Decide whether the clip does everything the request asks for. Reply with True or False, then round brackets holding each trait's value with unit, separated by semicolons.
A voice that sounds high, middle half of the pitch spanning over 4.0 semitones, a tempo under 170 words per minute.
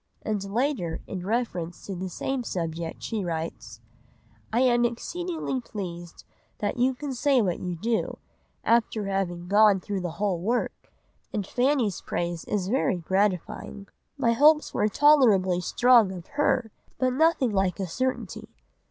True (205 Hz; 5.6 semitones; 145 wpm)